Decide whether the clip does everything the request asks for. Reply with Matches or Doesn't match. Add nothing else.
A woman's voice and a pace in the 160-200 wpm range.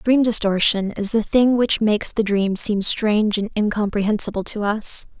Matches